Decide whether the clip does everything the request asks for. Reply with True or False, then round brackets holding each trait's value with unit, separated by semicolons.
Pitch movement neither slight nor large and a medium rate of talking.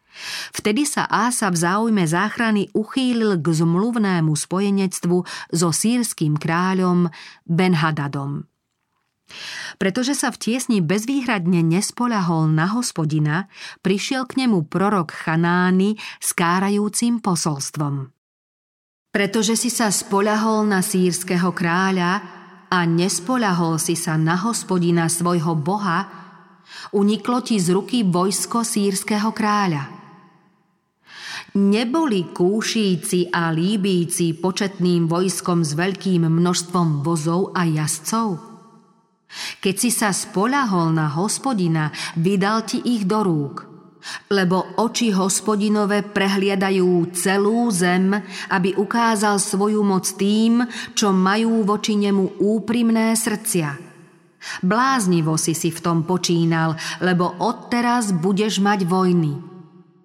False (3.6 semitones; 105 wpm)